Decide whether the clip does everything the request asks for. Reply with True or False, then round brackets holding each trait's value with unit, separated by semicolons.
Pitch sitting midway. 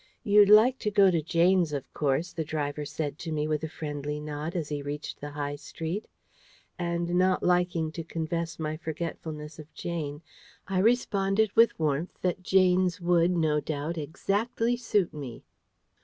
True (165 Hz)